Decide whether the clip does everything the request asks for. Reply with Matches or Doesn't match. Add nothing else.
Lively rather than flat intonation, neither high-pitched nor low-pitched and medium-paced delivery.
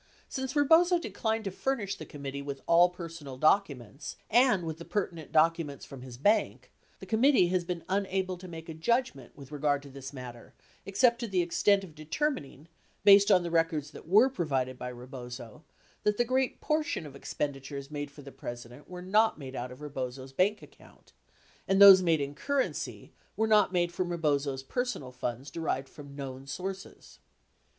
Matches